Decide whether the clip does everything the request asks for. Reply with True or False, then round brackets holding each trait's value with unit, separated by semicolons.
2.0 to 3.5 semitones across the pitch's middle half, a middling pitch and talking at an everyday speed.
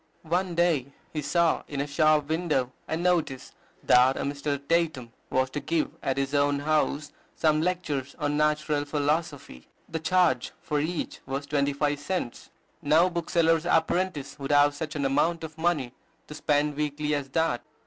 True (2.4 semitones; 150 Hz; 165 wpm)